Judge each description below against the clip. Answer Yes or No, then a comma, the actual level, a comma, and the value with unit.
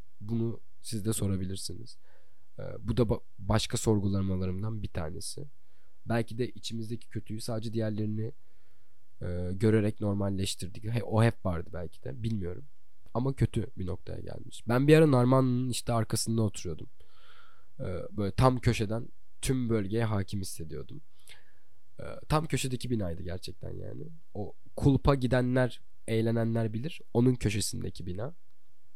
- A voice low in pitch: Yes, low, 110 Hz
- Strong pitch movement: No, average, 3.8 semitones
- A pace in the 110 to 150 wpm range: Yes, average, 115 wpm